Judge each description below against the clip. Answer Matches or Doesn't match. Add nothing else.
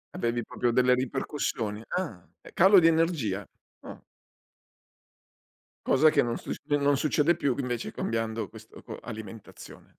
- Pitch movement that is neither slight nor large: Matches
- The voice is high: Doesn't match